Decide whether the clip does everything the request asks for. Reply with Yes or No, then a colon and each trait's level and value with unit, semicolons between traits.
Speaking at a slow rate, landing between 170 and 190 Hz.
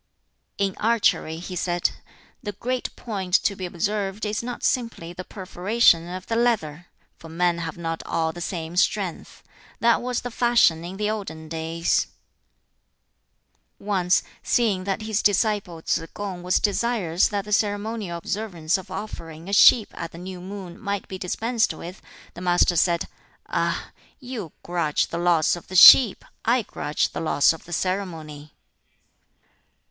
No: average, 155 wpm; medium, 185 Hz